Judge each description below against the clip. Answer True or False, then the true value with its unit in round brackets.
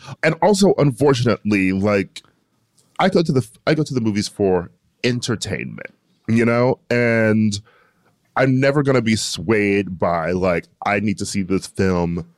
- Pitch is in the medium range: False (110 Hz)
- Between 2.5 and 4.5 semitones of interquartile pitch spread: False (5.0 semitones)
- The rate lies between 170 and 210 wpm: False (155 wpm)